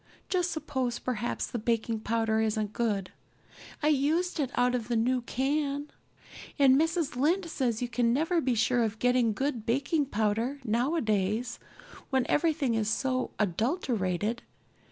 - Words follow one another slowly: No, average, 145 wpm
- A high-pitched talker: Yes, high, 245 Hz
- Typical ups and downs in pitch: Yes, average, 4.3 semitones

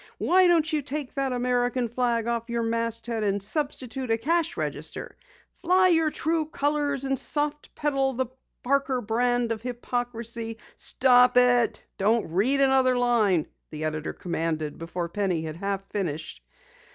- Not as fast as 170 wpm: Yes, average, 145 wpm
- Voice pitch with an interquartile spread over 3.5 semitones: Yes, average, 4.0 semitones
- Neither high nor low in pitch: No, high, 245 Hz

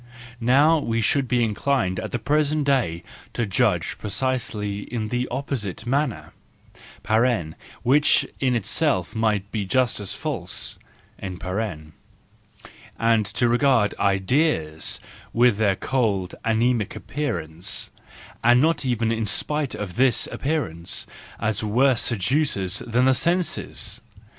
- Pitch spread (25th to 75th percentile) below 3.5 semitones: No, average, 4.7 semitones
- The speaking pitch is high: No, low, 115 Hz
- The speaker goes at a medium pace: No, slow, 120 wpm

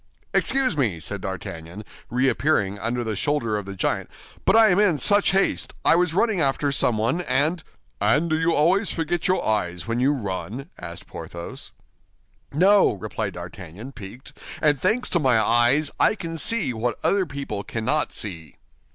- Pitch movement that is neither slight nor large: No, wide, 8.1 semitones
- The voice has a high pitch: No, low, 135 Hz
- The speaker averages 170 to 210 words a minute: No, average, 160 wpm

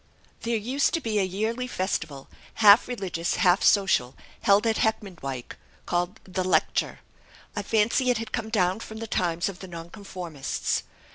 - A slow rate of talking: No, average, 155 wpm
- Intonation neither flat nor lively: Yes, average, 3.9 semitones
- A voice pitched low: No, high, 200 Hz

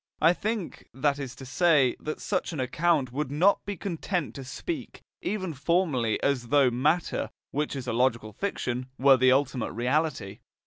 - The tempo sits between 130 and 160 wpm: No, average, 170 wpm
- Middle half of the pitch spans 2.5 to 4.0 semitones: No, average, 4.9 semitones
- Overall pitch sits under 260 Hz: Yes, medium, 140 Hz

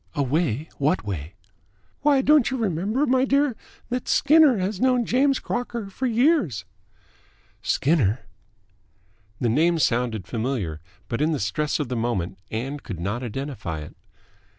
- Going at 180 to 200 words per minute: No, average, 145 wpm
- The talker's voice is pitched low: No, medium, 150 Hz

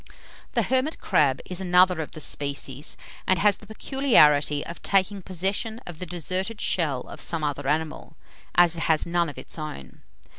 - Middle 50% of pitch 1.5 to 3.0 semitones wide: No, average, 4.1 semitones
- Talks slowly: No, average, 175 wpm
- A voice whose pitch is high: No, medium, 170 Hz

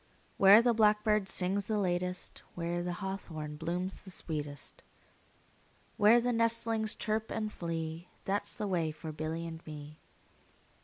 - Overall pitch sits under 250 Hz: Yes, medium, 185 Hz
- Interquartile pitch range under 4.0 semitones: No, average, 4.4 semitones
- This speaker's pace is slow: No, average, 150 wpm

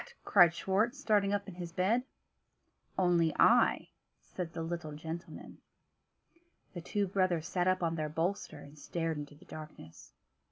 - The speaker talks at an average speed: Yes, average, 150 wpm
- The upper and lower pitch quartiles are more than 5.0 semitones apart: No, average, 2.8 semitones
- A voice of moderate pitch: Yes, medium, 175 Hz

